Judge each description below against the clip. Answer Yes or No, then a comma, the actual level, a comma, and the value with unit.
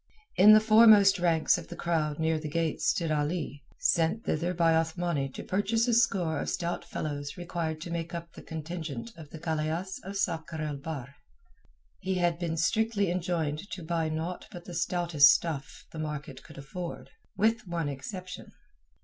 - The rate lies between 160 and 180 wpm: Yes, average, 170 wpm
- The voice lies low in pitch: No, medium, 165 Hz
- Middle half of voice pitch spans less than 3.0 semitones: Yes, narrow, 2.6 semitones